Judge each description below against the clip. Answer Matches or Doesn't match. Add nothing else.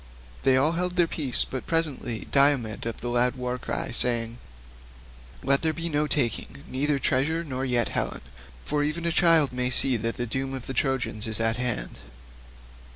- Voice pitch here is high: Doesn't match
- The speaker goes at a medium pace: Matches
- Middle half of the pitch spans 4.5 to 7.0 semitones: Doesn't match